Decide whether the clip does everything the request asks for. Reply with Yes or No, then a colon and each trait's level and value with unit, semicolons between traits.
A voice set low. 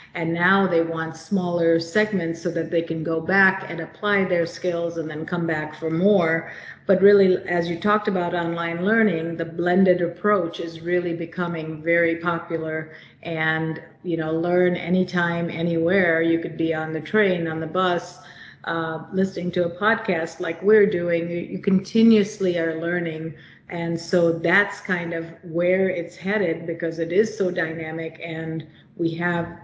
No: medium, 170 Hz